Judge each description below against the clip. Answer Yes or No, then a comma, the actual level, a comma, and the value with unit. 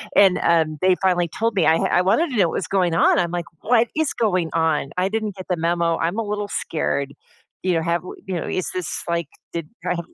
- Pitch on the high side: No, medium, 180 Hz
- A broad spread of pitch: No, average, 3.0 semitones